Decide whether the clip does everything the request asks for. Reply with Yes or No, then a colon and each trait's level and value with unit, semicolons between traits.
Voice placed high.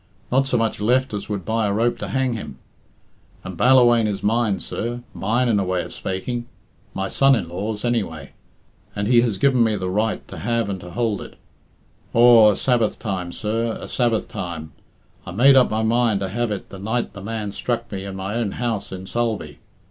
No: low, 110 Hz